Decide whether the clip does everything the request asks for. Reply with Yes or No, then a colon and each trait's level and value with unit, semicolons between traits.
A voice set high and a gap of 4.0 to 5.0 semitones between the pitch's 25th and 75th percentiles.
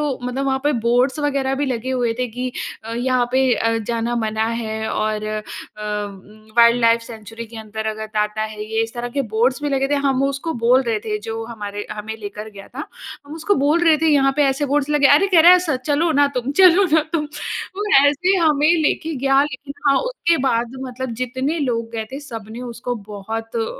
Yes: very high, 250 Hz; average, 4.3 semitones